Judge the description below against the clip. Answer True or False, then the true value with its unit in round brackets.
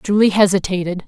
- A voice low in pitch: False (190 Hz)